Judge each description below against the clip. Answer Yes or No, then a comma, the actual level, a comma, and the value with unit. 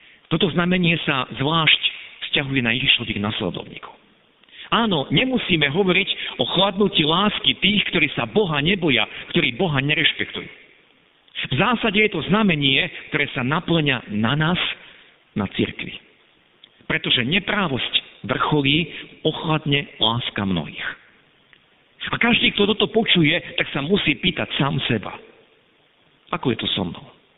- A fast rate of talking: No, average, 125 wpm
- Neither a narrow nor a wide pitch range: No, wide, 5.7 semitones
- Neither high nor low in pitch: Yes, medium, 155 Hz